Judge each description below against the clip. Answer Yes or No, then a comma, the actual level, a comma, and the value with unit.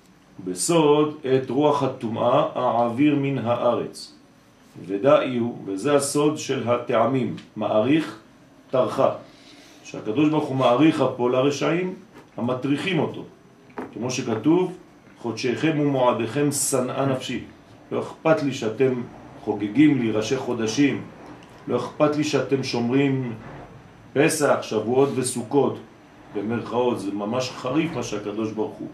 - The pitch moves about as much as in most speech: Yes, average, 3.5 semitones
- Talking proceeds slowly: Yes, slow, 110 wpm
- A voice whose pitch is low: Yes, low, 130 Hz